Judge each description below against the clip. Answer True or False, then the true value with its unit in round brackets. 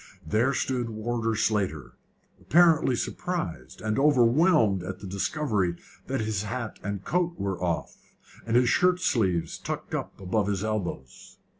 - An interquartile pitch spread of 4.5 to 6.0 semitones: True (5.5 semitones)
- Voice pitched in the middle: False (110 Hz)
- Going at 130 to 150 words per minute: True (135 wpm)